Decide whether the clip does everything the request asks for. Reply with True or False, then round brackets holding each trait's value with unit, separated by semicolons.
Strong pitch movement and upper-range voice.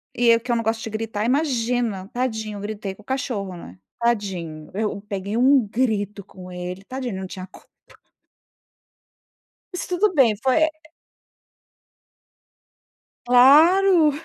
False (4.6 semitones; 225 Hz)